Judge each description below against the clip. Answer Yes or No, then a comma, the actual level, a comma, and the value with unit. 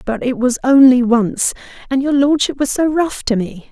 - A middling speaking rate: No, fast, 210 wpm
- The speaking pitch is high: Yes, very high, 255 Hz